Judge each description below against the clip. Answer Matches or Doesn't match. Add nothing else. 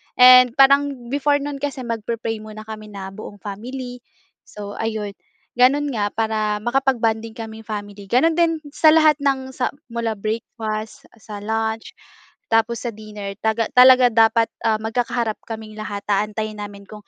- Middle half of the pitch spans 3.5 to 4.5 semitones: Doesn't match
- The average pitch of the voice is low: Doesn't match